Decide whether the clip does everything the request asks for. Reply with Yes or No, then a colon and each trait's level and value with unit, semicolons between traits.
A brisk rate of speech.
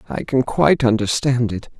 No: average, 165 wpm